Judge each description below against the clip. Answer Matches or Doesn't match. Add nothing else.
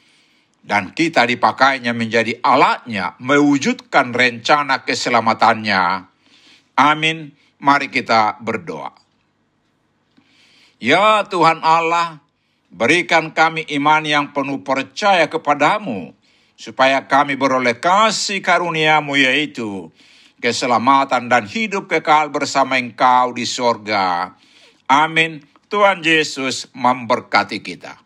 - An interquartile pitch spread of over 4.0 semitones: Matches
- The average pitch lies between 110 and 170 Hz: Matches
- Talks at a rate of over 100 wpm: Doesn't match